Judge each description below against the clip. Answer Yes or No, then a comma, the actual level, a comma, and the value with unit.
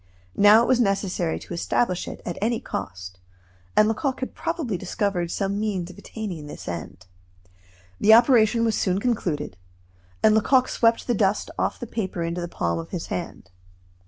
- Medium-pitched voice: No, high, 200 Hz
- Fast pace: No, average, 170 wpm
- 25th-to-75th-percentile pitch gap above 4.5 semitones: Yes, average, 5.0 semitones